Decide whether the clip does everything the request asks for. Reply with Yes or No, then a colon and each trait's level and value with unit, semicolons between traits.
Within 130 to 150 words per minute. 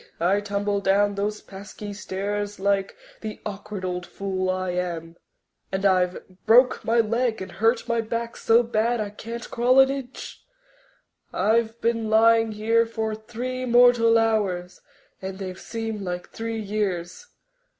Yes: average, 145 wpm